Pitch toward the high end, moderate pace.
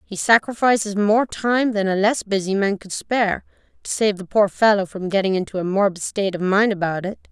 No: high, 200 Hz; fast, 215 wpm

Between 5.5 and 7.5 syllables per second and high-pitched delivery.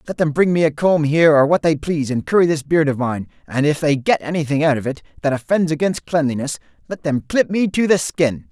No: 5.9 syllables/s; medium, 150 Hz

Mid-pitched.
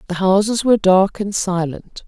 No: high, 195 Hz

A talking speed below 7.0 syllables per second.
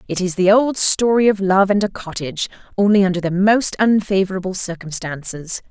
Yes: 5.4 syllables/s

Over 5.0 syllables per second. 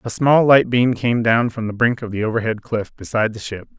Yes: 5.6 syllables/s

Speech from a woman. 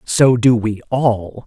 Yes: female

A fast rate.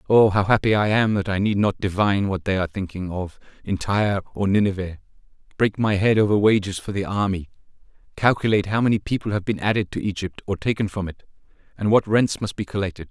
Yes: fast, 210 wpm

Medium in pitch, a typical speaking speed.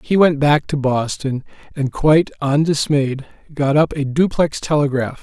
Yes: medium, 145 Hz; average, 150 wpm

